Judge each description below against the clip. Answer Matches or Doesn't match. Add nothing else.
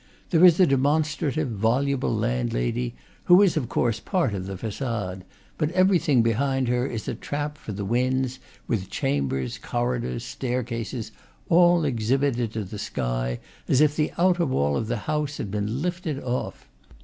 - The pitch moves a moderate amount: Doesn't match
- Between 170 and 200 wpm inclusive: Doesn't match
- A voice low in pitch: Matches